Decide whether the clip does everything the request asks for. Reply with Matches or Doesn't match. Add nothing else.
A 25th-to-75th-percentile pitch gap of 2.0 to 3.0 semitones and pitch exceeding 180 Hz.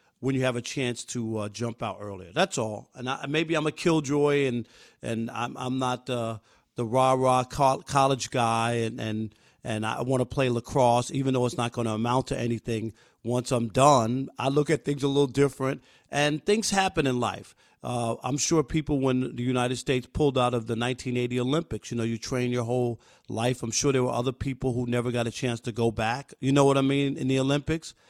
Doesn't match